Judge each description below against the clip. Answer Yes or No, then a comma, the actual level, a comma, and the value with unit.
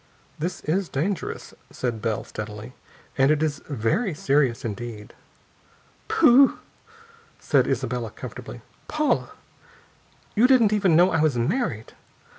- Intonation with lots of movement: Yes, wide, 7.9 semitones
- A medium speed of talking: No, slow, 115 wpm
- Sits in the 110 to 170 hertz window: Yes, medium, 140 Hz